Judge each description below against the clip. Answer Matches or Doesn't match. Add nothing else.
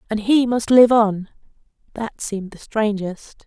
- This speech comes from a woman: Matches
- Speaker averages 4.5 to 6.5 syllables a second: Doesn't match